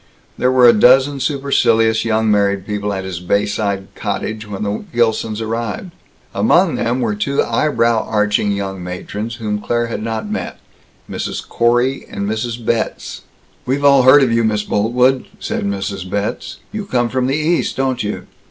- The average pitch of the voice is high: No, low, 115 Hz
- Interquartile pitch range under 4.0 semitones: Yes, average, 3.5 semitones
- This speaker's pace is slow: No, average, 165 wpm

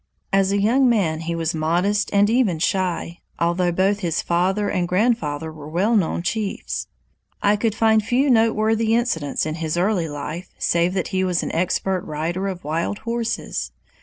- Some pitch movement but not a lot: Yes, average, 4.2 semitones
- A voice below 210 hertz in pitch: Yes, medium, 185 Hz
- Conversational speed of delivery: Yes, average, 170 wpm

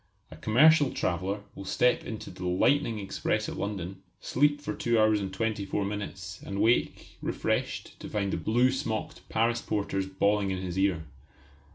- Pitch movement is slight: No, average, 3.2 semitones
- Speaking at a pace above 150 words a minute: Yes, average, 170 wpm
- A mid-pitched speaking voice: No, low, 105 Hz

